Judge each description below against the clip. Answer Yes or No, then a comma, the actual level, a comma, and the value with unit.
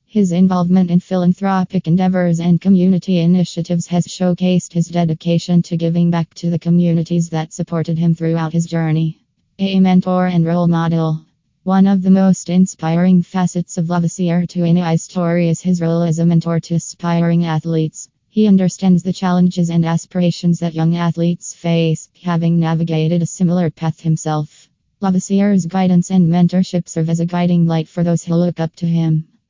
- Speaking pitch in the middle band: Yes, medium, 170 Hz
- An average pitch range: No, narrow, 1.5 semitones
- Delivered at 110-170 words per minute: Yes, average, 165 wpm